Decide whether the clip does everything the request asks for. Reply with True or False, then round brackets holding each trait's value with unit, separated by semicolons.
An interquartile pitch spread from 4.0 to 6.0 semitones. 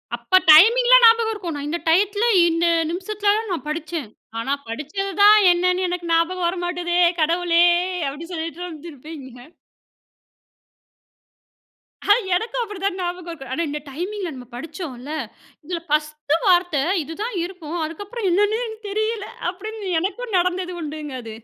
True (4.5 semitones)